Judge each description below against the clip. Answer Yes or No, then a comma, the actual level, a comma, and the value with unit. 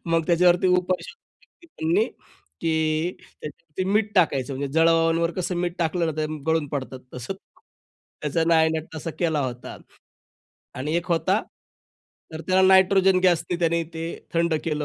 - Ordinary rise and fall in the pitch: No, narrow, 2.3 semitones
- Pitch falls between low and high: Yes, medium, 165 Hz